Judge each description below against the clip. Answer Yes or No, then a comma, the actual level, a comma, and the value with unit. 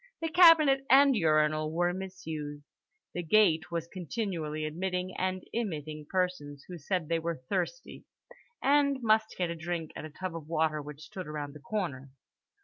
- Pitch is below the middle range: No, medium, 170 Hz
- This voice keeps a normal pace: Yes, average, 160 wpm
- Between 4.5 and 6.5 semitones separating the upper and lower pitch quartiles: No, average, 3.8 semitones